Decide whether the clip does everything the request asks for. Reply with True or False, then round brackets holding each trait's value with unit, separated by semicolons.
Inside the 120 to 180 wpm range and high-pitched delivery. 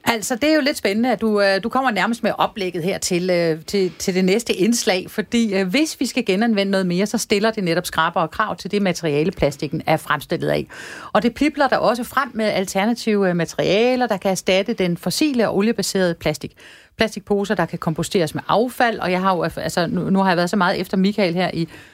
False (210 wpm; 195 Hz)